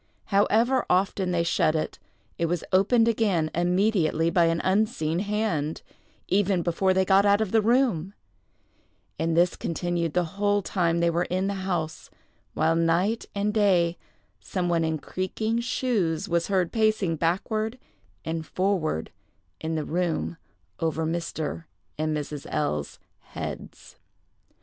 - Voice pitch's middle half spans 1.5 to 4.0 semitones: Yes, average, 3.7 semitones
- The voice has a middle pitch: Yes, medium, 180 Hz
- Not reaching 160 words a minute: Yes, average, 140 wpm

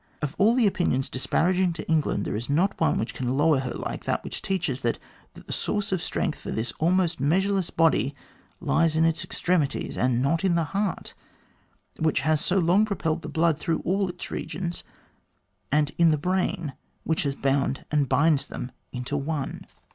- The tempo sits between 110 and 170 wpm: No, average, 185 wpm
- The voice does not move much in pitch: No, average, 4.2 semitones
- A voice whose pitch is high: No, medium, 160 Hz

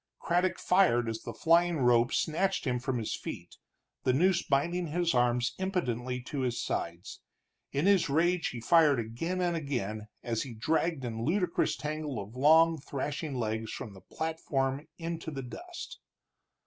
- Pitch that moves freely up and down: Yes, wide, 5.7 semitones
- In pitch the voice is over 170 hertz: No, medium, 140 Hz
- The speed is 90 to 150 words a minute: No, average, 160 wpm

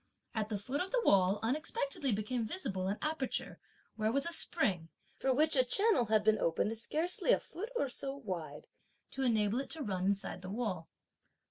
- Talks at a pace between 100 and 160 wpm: No, average, 190 wpm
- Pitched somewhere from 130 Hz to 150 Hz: No, high, 230 Hz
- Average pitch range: No, wide, 5.9 semitones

